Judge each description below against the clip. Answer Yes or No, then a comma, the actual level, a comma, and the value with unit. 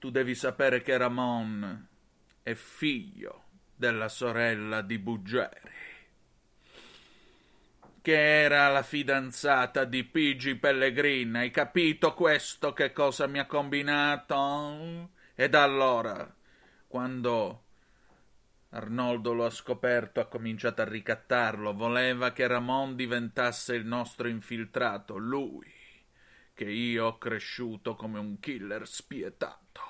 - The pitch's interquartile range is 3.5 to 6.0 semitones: No, average, 3.0 semitones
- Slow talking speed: Yes, slow, 110 wpm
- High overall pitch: No, low, 125 Hz